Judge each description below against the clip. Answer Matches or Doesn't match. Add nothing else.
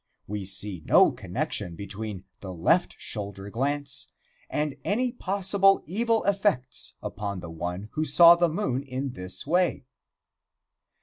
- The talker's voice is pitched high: Doesn't match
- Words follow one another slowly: Matches